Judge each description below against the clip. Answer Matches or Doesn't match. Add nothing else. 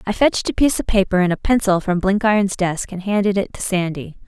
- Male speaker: Doesn't match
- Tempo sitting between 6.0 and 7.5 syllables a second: Matches